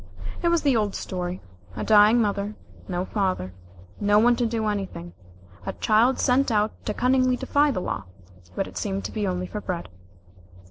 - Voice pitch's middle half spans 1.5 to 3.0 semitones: No, average, 4.1 semitones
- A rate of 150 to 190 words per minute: Yes, average, 180 wpm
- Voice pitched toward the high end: Yes, high, 210 Hz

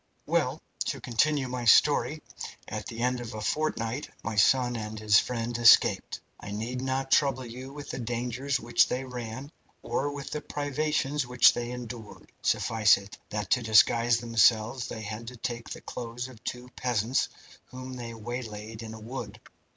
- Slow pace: No, average, 170 wpm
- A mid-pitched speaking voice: No, low, 120 Hz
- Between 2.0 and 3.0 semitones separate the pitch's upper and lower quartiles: Yes, narrow, 2.5 semitones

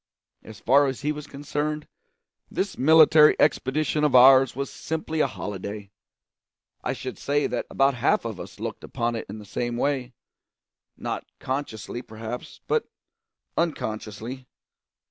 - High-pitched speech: No, low, 130 Hz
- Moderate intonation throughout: Yes, average, 4.0 semitones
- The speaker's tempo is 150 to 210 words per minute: No, average, 140 wpm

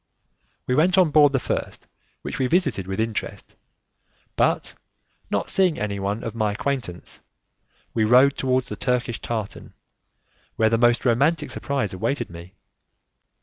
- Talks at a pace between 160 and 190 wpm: No, average, 140 wpm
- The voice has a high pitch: No, low, 120 Hz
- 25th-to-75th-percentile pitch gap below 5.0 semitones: Yes, average, 4.6 semitones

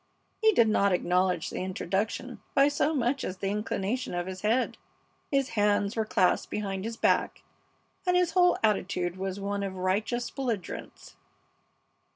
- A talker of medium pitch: No, high, 205 Hz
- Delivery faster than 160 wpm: No, average, 155 wpm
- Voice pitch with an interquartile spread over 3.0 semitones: Yes, average, 4.5 semitones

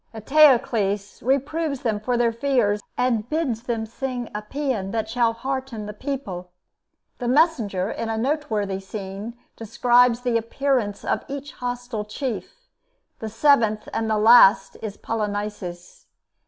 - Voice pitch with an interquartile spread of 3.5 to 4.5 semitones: Yes, average, 3.8 semitones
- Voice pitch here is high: Yes, high, 230 Hz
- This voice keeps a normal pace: No, slow, 130 wpm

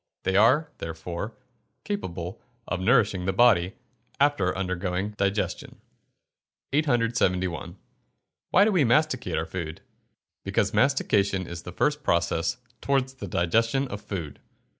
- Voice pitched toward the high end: No, low, 100 Hz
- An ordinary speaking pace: No, slow, 120 wpm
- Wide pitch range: Yes, wide, 6.3 semitones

